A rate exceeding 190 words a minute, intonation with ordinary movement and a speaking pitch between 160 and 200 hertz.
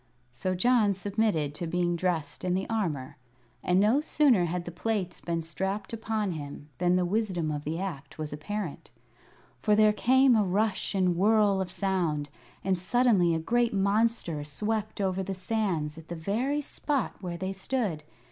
No: average, 170 wpm; average, 4.1 semitones; high, 190 Hz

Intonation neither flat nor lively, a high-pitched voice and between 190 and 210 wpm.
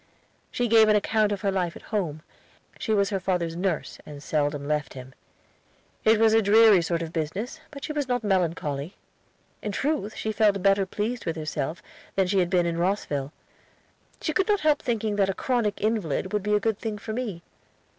Yes: average, 4.6 semitones; high, 200 Hz; average, 200 wpm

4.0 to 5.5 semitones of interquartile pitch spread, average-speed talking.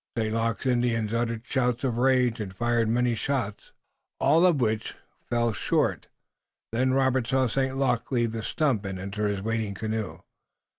No: average, 2.8 semitones; average, 160 wpm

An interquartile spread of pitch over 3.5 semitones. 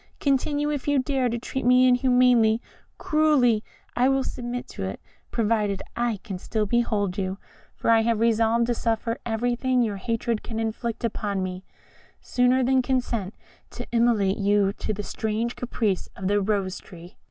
No: average, 3.2 semitones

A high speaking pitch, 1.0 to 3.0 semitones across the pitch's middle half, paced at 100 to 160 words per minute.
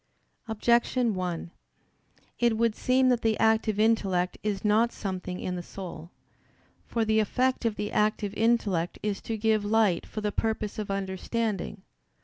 Yes: high, 215 Hz; narrow, 2.6 semitones; average, 150 wpm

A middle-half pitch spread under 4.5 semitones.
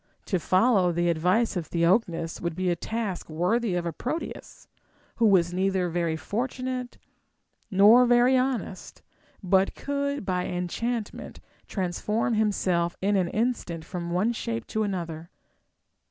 No: average, 5.0 semitones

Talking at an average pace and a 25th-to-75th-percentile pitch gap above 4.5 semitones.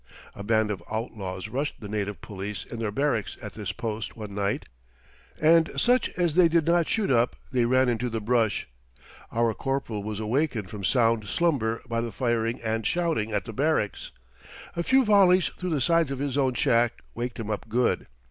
Yes: average, 190 wpm; average, 5.2 semitones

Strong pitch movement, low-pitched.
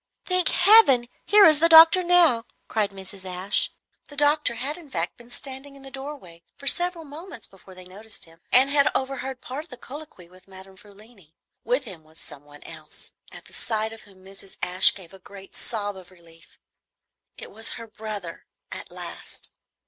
No: wide, 7.1 semitones; high, 225 Hz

